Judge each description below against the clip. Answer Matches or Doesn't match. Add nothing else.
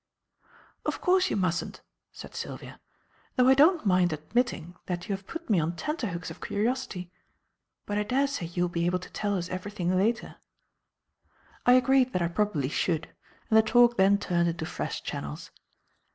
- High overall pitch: Matches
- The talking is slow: Doesn't match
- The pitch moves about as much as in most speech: Doesn't match